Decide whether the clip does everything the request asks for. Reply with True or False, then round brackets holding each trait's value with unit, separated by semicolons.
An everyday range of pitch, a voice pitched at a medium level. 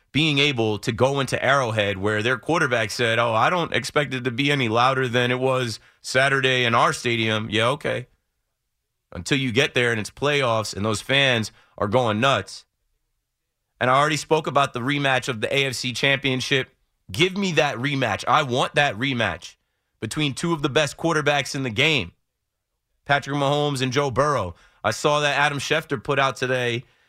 False (3.3 semitones; 130 Hz)